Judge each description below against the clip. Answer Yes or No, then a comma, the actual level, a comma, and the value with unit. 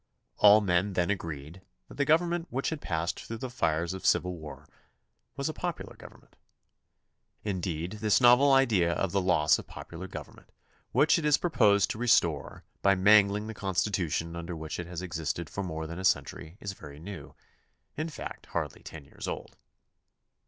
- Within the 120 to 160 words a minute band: No, average, 175 wpm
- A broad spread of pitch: No, average, 4.3 semitones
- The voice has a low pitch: Yes, very low, 95 Hz